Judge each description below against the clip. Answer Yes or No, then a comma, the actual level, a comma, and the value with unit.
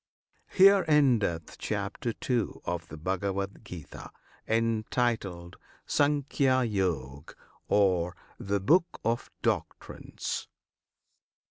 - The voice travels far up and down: Yes, wide, 6.2 semitones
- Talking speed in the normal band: No, slow, 85 wpm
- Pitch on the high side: No, low, 105 Hz